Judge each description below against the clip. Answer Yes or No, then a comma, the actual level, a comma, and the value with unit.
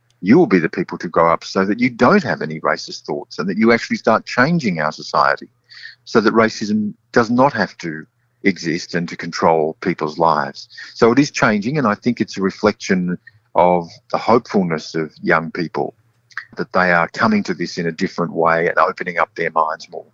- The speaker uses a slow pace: No, fast, 205 wpm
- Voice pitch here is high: No, low, 100 Hz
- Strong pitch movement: Yes, wide, 5.7 semitones